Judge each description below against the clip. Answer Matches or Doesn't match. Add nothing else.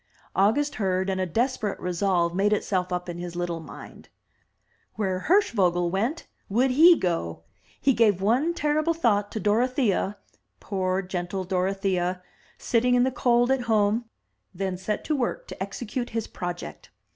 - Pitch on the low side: Doesn't match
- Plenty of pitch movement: Doesn't match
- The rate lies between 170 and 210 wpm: Doesn't match